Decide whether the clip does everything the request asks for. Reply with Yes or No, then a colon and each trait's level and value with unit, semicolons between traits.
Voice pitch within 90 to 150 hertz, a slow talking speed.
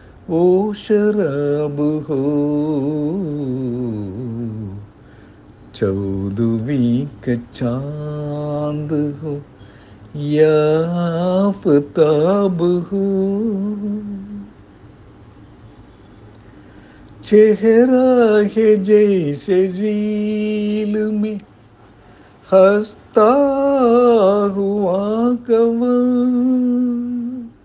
No: medium, 180 Hz; slow, 35 wpm